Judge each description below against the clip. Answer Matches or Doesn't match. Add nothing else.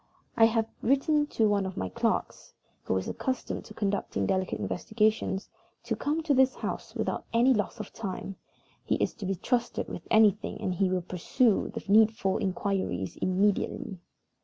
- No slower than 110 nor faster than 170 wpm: Matches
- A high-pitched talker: Matches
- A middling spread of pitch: Matches